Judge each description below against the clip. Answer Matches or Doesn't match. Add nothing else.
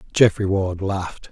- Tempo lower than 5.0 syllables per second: Matches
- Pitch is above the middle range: Doesn't match